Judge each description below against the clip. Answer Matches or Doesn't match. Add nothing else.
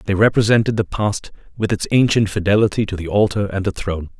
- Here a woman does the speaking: Doesn't match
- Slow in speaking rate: Doesn't match